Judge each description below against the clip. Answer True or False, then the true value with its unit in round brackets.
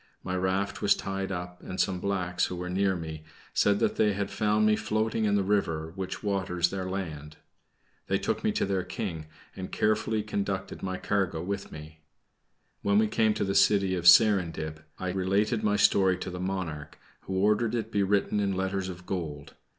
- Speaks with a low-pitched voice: True (95 Hz)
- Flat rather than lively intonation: True (2.3 semitones)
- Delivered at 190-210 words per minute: True (195 wpm)